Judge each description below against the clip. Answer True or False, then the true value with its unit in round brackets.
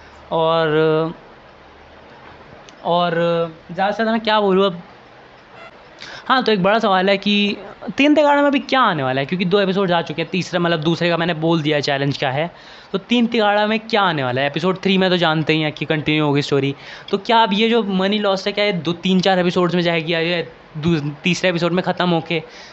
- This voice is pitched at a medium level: True (175 Hz)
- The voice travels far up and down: False (3.6 semitones)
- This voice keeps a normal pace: False (215 wpm)